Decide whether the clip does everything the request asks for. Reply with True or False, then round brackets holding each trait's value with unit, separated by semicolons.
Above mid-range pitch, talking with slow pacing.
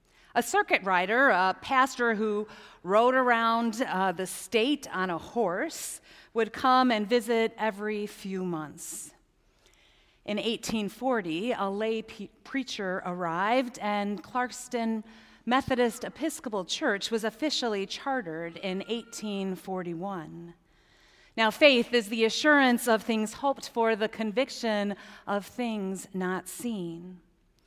True (220 Hz; 115 wpm)